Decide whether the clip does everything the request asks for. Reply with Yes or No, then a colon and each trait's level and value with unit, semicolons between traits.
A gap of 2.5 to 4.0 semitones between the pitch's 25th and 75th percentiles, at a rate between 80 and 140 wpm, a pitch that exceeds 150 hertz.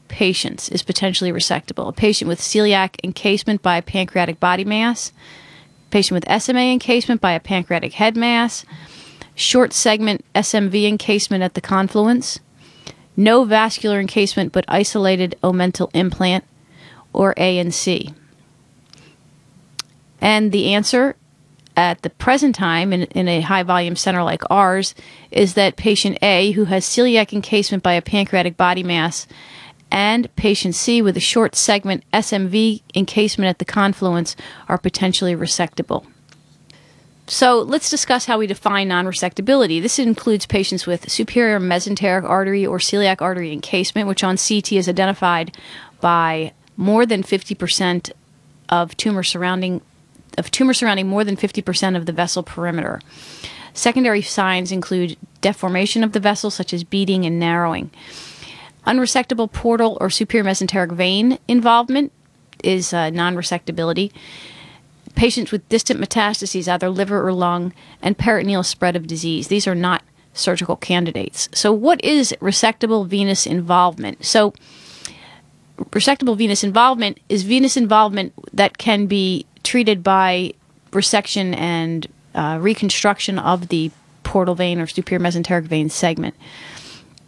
Yes: average, 3.2 semitones; slow, 135 wpm; high, 190 Hz